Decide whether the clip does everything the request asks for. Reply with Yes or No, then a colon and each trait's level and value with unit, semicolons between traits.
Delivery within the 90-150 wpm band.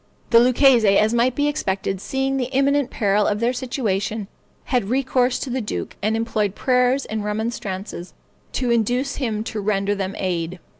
No: average, 165 wpm